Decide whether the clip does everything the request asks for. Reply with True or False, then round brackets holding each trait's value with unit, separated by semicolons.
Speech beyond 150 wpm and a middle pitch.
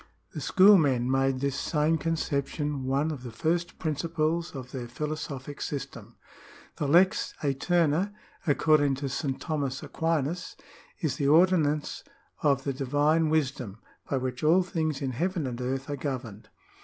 False (145 wpm; 145 Hz)